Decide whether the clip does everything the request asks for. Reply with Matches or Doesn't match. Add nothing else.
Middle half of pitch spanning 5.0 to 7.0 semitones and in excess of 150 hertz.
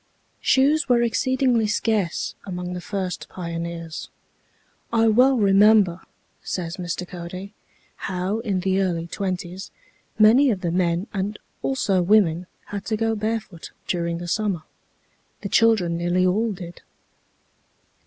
Doesn't match